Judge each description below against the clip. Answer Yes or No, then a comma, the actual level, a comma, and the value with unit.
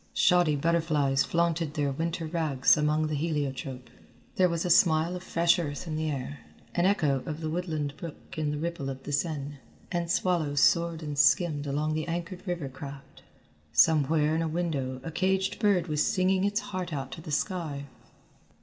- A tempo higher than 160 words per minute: Yes, average, 180 wpm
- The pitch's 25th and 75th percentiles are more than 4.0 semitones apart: No, average, 3.0 semitones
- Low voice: No, medium, 160 Hz